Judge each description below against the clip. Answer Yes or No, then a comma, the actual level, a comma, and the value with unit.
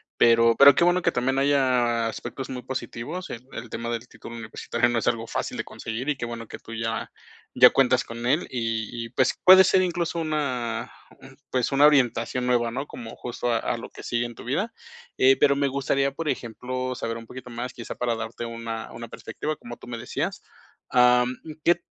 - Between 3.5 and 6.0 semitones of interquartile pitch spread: No, average, 2.9 semitones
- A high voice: No, low, 125 Hz